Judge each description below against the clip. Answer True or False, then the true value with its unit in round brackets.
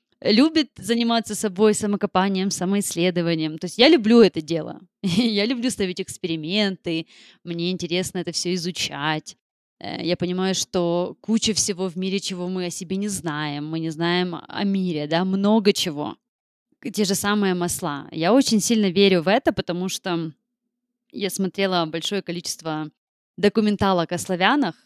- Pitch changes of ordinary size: True (3.3 semitones)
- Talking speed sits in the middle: True (145 wpm)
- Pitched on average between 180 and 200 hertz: True (190 Hz)